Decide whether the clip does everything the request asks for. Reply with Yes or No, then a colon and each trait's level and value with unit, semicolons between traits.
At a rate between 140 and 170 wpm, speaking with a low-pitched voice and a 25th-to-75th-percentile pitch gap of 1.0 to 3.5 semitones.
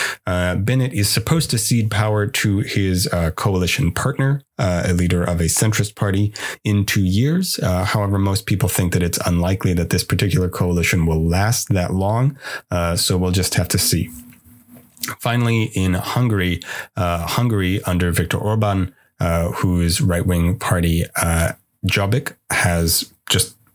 No: average, 155 wpm; very low, 95 Hz; average, 4.2 semitones